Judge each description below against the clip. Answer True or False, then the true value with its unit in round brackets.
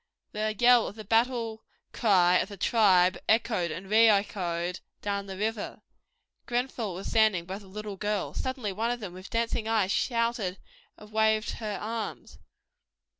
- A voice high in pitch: True (215 Hz)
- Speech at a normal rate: True (160 wpm)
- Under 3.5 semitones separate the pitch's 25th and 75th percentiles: True (2.9 semitones)